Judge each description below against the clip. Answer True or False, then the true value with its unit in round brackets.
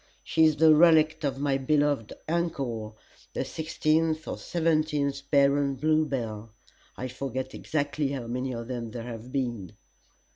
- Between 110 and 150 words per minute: True (140 wpm)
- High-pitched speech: False (140 Hz)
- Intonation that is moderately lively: True (3.9 semitones)